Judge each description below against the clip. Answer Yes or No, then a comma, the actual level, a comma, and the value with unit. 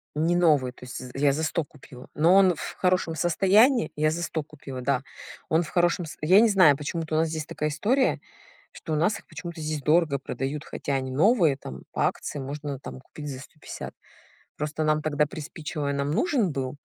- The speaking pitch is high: No, medium, 155 Hz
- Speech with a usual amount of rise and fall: Yes, average, 3.3 semitones